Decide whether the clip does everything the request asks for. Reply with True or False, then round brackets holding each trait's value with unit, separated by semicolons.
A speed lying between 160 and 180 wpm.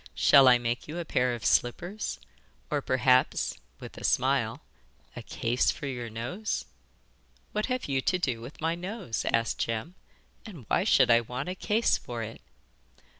True (170 wpm)